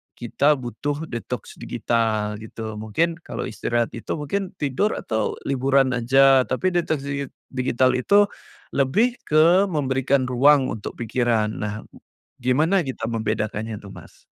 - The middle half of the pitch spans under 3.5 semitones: No, average, 4.3 semitones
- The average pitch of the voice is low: Yes, low, 130 Hz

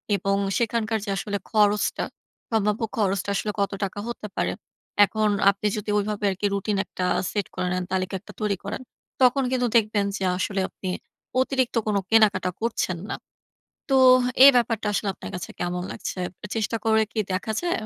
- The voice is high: Yes, high, 210 Hz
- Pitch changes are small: Yes, narrow, 2.2 semitones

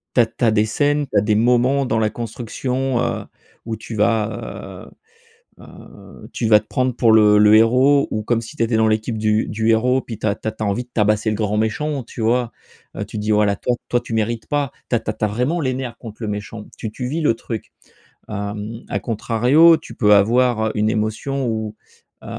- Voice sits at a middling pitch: No, low, 115 Hz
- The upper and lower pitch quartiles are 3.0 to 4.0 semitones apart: No, narrow, 2.5 semitones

